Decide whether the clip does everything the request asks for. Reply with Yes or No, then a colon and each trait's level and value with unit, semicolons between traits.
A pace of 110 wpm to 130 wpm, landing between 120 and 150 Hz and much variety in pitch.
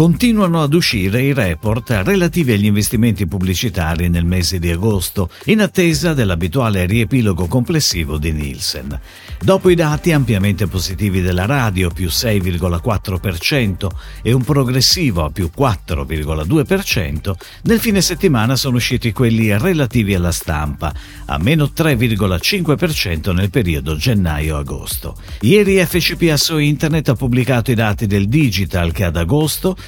No: average, 125 wpm; low, 105 Hz; wide, 8.2 semitones